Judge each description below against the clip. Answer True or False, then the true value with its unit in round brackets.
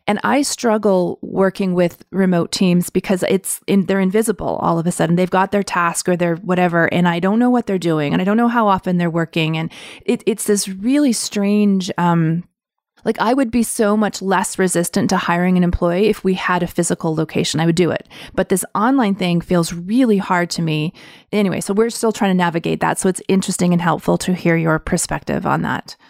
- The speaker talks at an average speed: False (220 wpm)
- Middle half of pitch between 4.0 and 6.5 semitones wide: False (3.1 semitones)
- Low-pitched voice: False (190 Hz)